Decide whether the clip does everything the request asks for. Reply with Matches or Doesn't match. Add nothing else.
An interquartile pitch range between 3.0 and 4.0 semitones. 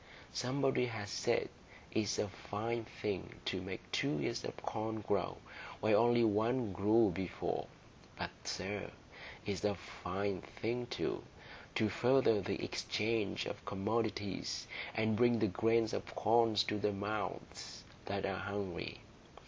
Doesn't match